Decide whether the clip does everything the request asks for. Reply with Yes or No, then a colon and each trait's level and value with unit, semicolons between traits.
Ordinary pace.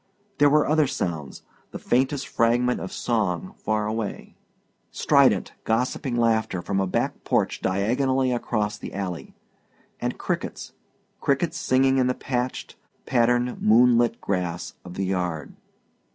No: slow, 130 wpm